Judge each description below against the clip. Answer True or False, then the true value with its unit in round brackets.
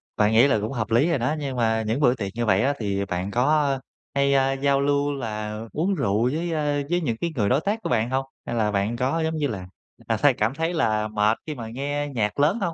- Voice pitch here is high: False (130 Hz)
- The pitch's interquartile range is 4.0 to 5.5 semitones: True (5.1 semitones)